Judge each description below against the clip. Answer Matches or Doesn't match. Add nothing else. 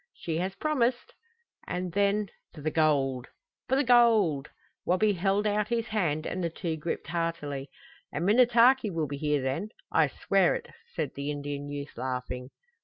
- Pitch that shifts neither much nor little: Doesn't match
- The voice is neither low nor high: Matches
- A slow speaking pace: Doesn't match